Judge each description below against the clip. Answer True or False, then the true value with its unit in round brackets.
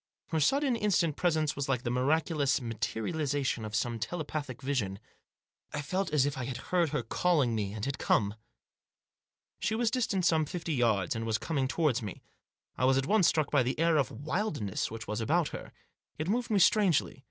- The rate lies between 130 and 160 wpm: False (195 wpm)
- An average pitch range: False (6.0 semitones)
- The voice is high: False (145 Hz)